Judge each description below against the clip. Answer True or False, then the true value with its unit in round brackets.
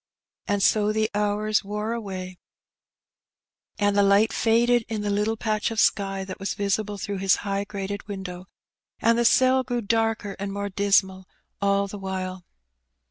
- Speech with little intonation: True (1.7 semitones)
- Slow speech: False (160 wpm)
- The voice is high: True (205 Hz)